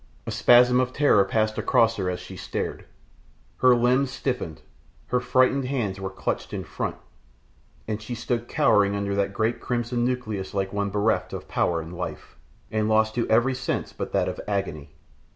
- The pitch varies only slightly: No, average, 3.8 semitones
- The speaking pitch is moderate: No, low, 110 Hz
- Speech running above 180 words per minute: No, average, 175 wpm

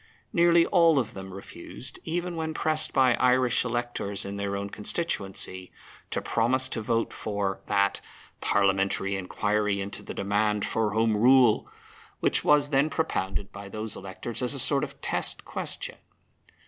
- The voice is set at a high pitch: No, low, 110 Hz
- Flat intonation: No, average, 5.0 semitones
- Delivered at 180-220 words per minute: No, average, 150 wpm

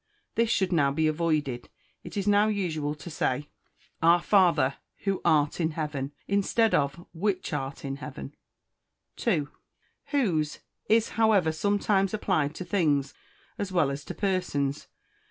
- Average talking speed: Yes, average, 145 wpm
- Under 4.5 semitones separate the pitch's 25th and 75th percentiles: No, average, 5.3 semitones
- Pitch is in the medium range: Yes, medium, 165 Hz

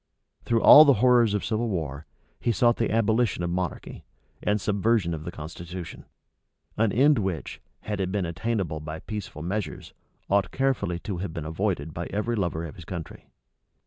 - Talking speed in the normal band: Yes, average, 175 wpm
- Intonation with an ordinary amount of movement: Yes, average, 4.8 semitones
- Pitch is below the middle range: Yes, very low, 95 Hz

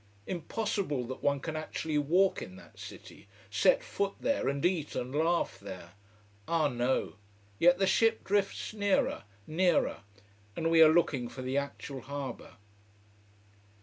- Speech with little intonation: No, average, 5.3 semitones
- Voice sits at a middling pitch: Yes, medium, 160 Hz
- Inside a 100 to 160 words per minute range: Yes, average, 145 wpm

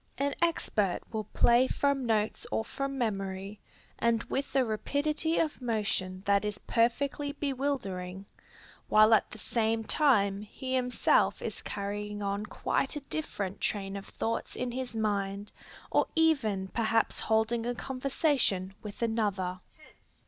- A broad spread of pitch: No, average, 4.6 semitones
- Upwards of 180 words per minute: No, slow, 135 wpm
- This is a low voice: No, high, 225 Hz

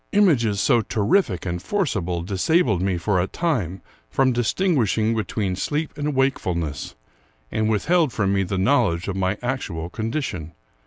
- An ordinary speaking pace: Yes, average, 150 wpm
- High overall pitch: No, low, 110 Hz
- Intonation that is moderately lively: No, wide, 6.6 semitones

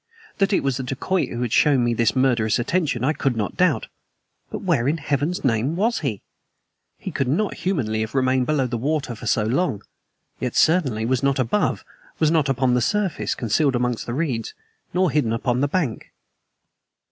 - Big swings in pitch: No, average, 4.5 semitones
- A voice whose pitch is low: Yes, low, 130 Hz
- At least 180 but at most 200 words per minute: Yes, average, 190 wpm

